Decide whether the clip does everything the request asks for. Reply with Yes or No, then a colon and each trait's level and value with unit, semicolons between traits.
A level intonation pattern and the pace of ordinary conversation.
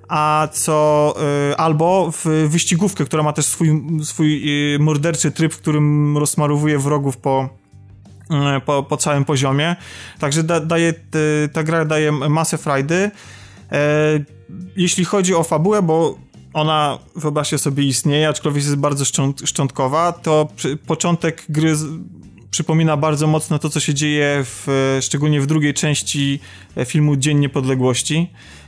Yes: narrow, 2.1 semitones; average, 130 wpm